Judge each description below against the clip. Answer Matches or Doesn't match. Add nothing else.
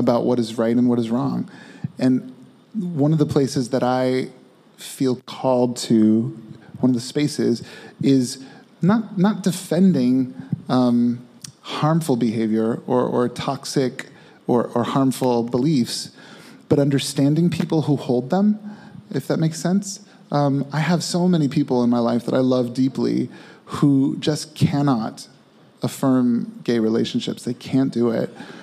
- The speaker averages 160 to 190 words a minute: Doesn't match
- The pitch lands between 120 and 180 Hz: Matches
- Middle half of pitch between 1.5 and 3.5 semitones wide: Doesn't match